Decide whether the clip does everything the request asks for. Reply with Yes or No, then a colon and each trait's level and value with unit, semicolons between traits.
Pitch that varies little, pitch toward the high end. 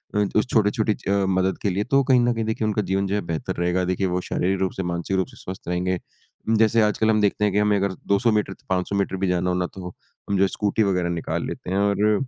No: narrow, 2.3 semitones; low, 100 Hz